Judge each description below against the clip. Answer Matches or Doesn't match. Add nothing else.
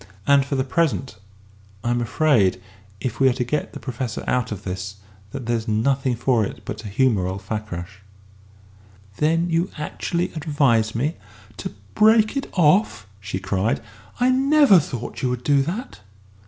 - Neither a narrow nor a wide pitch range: Doesn't match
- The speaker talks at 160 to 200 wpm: Matches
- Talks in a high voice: Doesn't match